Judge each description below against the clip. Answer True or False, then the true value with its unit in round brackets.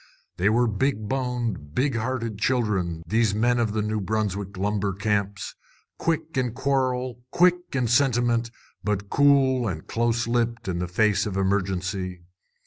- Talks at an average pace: True (145 wpm)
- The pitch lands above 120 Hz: False (110 Hz)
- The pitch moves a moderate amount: True (3.9 semitones)